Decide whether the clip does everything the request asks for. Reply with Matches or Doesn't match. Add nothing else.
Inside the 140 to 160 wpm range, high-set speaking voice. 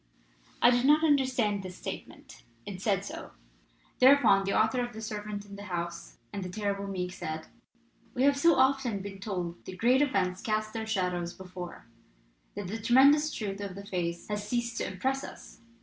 Doesn't match